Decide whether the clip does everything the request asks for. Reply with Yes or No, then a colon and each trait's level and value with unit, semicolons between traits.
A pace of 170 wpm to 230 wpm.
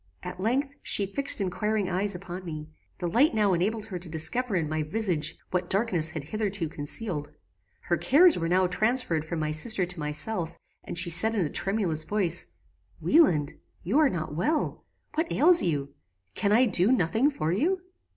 Yes: average, 180 wpm